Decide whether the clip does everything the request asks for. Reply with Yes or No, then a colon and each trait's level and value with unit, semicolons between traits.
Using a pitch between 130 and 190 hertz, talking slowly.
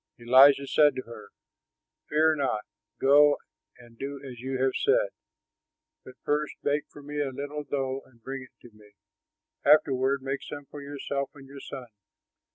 No: low, 135 Hz; average, 165 wpm